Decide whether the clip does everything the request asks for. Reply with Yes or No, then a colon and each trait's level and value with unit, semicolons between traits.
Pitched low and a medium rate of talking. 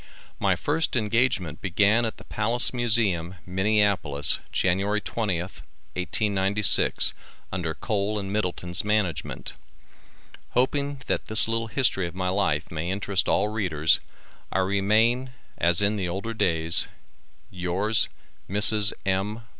No: low, 100 Hz; slow, 120 wpm